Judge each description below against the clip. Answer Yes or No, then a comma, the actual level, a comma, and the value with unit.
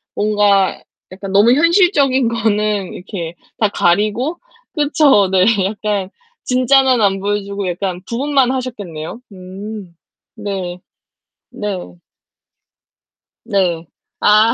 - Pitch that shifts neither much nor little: Yes, average, 4.5 semitones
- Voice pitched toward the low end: No, high, 205 Hz